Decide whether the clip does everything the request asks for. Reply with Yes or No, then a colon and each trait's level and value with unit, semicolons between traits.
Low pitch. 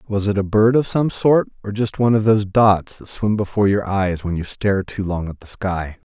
Yes: low, 100 Hz